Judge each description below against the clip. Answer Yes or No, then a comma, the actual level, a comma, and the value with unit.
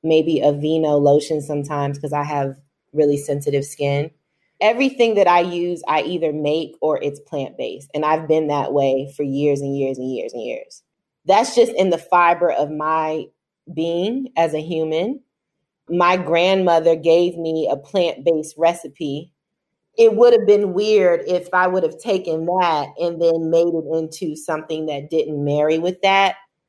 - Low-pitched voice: No, medium, 160 Hz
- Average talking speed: Yes, average, 170 wpm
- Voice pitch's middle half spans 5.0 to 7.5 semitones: No, average, 3.3 semitones